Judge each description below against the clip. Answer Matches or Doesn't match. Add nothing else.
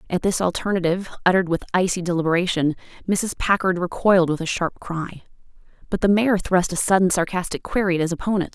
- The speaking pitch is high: Doesn't match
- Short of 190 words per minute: Matches